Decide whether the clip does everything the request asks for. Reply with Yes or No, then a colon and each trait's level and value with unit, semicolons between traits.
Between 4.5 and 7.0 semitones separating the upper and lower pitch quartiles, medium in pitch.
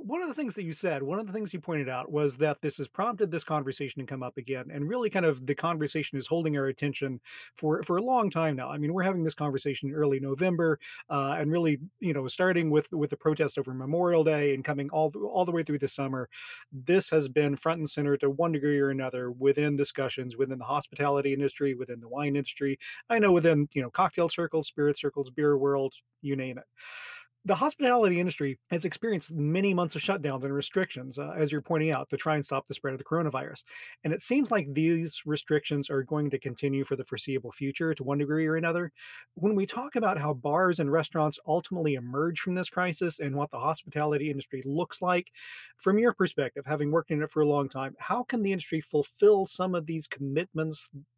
No: average, 4.0 semitones; medium, 150 Hz